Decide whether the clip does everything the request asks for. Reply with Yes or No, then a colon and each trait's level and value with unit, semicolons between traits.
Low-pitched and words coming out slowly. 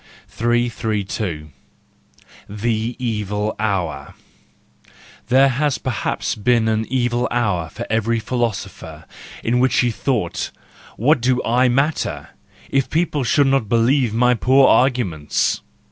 Yes: low, 120 Hz; slow, 115 wpm